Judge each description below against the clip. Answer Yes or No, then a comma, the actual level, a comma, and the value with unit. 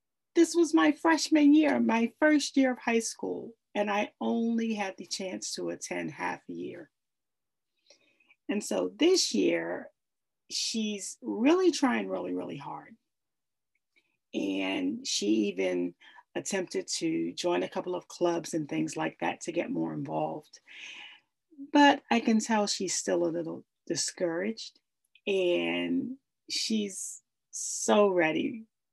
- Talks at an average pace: No, slow, 130 wpm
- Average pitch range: No, wide, 7.9 semitones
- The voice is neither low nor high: No, high, 215 Hz